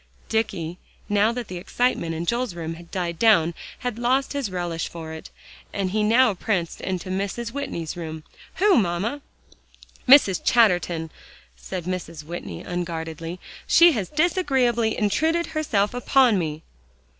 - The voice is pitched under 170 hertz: No, high, 195 Hz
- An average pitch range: No, wide, 6.2 semitones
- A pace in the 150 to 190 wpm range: No, average, 140 wpm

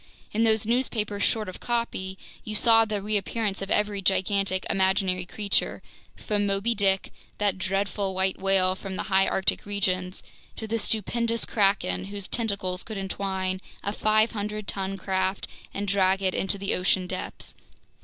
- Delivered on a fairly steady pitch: Yes, narrow, 1.9 semitones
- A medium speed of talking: Yes, average, 155 wpm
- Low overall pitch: No, high, 200 Hz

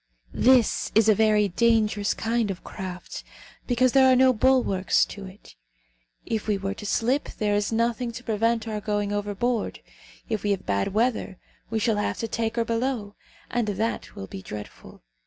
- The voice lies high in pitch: Yes, high, 220 Hz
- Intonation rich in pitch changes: No, narrow, 2.5 semitones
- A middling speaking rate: Yes, average, 175 wpm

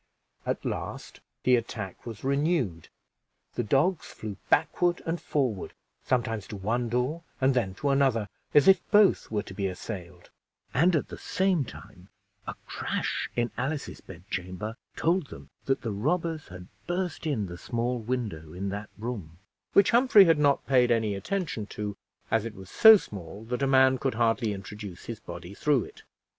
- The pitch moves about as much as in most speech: No, wide, 6.1 semitones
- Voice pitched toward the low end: Yes, low, 120 Hz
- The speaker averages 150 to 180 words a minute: Yes, average, 170 wpm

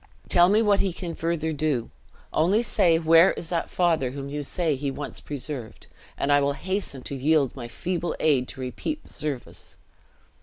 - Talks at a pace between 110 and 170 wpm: No, average, 185 wpm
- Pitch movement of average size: Yes, average, 3.8 semitones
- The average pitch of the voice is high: No, medium, 155 Hz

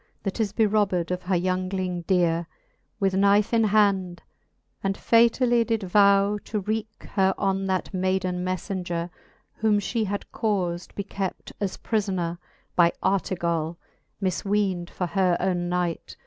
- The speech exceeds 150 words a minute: No, slow, 135 wpm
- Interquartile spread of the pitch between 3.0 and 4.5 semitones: No, narrow, 2.4 semitones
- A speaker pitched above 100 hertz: Yes, high, 190 Hz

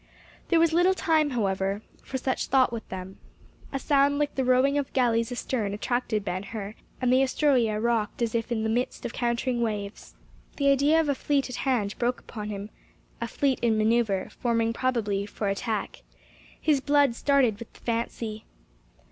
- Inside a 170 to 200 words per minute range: Yes, average, 175 wpm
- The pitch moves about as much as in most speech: Yes, average, 3.9 semitones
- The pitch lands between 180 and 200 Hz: No, high, 235 Hz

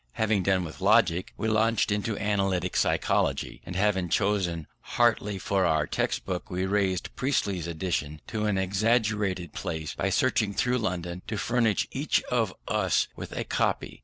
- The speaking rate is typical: Yes, average, 160 wpm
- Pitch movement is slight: No, average, 3.0 semitones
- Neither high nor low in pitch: No, very low, 95 Hz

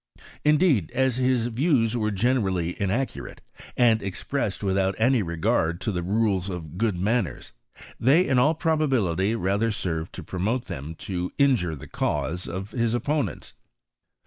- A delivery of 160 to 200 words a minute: No, average, 145 wpm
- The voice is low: Yes, low, 110 Hz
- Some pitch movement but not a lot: No, wide, 5.7 semitones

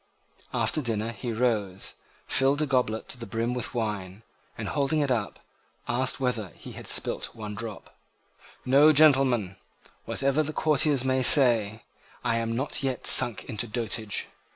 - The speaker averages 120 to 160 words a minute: Yes, average, 155 wpm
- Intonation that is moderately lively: Yes, average, 3.6 semitones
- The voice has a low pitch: Yes, low, 120 Hz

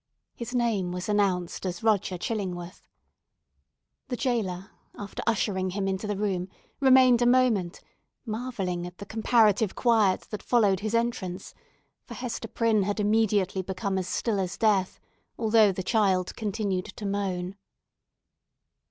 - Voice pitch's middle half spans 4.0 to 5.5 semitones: No, average, 3.2 semitones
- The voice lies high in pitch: Yes, high, 205 Hz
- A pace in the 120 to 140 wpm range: Yes, slow, 135 wpm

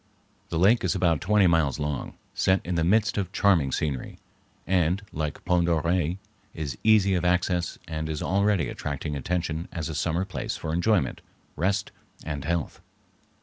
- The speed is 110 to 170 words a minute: Yes, average, 160 wpm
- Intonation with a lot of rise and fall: No, average, 3.2 semitones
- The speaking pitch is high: No, very low, 85 Hz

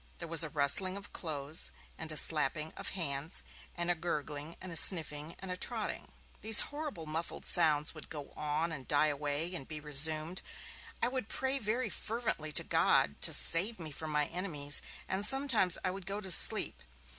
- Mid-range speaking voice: Yes, medium, 165 Hz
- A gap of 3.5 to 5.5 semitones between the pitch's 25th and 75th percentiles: Yes, average, 4.1 semitones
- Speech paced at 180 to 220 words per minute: Yes, average, 185 wpm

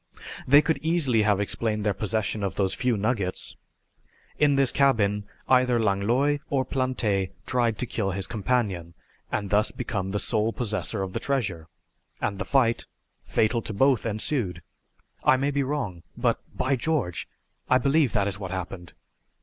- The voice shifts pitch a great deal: No, average, 4.7 semitones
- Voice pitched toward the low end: Yes, low, 110 Hz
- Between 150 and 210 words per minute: Yes, average, 160 wpm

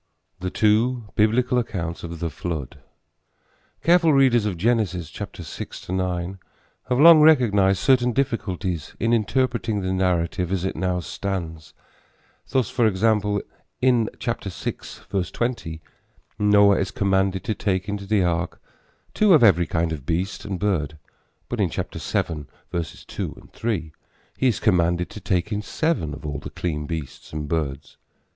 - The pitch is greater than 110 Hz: No, very low, 95 Hz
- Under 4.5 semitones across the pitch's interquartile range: No, average, 5.0 semitones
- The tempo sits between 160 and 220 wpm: No, average, 140 wpm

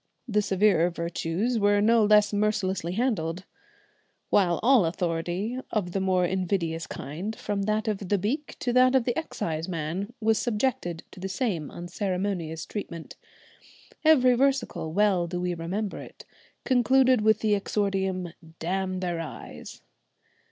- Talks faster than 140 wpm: No, slow, 135 wpm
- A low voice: No, high, 195 Hz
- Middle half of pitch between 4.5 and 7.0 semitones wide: No, average, 3.8 semitones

